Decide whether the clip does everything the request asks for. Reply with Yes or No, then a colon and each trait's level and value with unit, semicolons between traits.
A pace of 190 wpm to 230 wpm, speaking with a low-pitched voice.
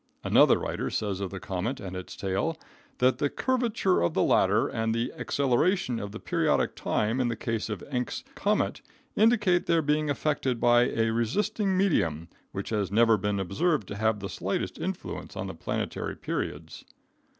No: average, 170 wpm; low, 115 Hz